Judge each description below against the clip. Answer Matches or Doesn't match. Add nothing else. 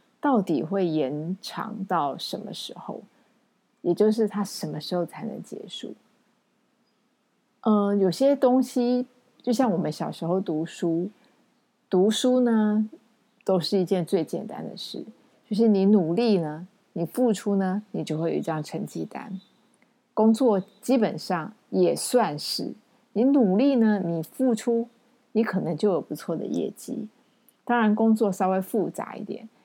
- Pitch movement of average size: Matches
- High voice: Matches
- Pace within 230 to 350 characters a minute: Doesn't match